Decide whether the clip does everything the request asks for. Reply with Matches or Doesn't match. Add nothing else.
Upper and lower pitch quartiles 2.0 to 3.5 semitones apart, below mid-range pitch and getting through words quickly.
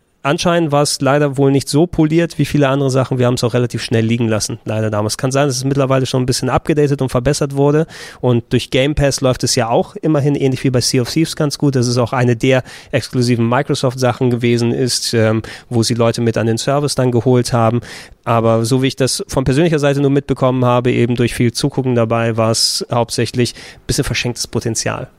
Matches